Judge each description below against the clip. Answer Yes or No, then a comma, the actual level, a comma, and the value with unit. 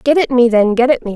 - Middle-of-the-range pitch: No, high, 245 Hz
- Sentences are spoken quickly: Yes, fast, 365 wpm